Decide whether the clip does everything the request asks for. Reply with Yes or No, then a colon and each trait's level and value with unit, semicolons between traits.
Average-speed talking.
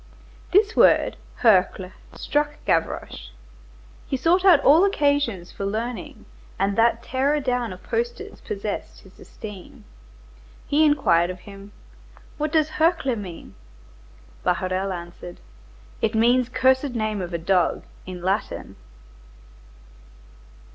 No: slow, 115 wpm